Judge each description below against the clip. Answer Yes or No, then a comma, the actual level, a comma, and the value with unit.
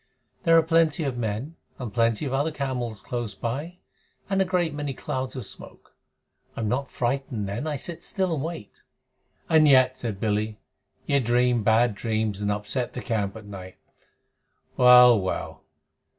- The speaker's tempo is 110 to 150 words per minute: No, average, 165 wpm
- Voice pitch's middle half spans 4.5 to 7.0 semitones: Yes, average, 5.0 semitones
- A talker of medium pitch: No, low, 125 Hz